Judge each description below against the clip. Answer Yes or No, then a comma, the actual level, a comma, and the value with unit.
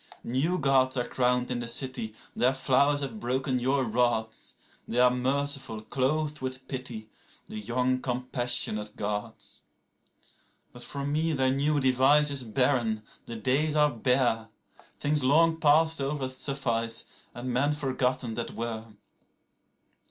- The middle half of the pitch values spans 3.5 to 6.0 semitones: No, average, 2.8 semitones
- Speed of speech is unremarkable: No, slow, 125 wpm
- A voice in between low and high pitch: No, low, 130 Hz